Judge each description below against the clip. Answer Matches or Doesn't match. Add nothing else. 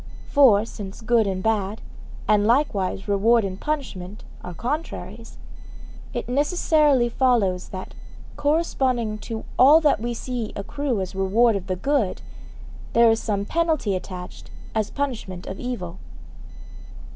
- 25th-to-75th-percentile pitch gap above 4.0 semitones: Matches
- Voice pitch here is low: Doesn't match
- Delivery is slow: Matches